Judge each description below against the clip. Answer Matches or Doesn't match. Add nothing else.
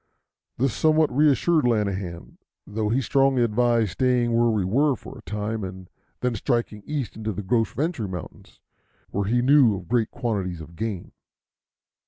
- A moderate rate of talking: Matches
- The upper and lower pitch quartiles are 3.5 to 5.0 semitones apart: Matches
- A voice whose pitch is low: Matches